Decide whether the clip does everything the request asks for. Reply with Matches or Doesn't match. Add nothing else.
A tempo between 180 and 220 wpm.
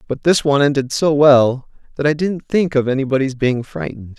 Matches